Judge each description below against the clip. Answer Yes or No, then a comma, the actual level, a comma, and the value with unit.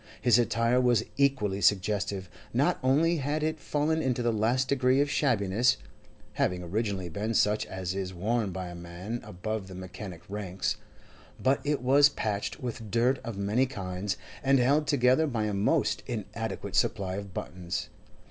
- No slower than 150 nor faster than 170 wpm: Yes, average, 160 wpm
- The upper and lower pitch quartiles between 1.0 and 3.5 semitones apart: No, average, 5.3 semitones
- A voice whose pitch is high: No, low, 110 Hz